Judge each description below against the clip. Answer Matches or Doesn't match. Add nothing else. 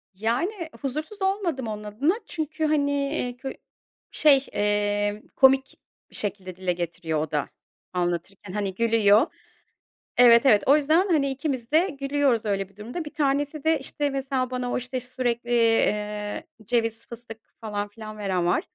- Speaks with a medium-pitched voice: Doesn't match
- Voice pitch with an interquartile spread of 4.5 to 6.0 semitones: Matches